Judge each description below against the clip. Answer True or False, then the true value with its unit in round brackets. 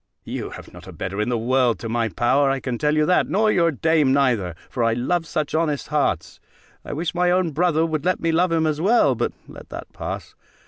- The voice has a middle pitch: True (150 Hz)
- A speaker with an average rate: False (235 wpm)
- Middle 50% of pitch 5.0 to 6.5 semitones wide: True (5.3 semitones)